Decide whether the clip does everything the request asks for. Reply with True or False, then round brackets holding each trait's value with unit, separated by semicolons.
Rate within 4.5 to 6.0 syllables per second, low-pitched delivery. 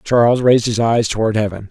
False (6.2 syllables/s; 115 Hz)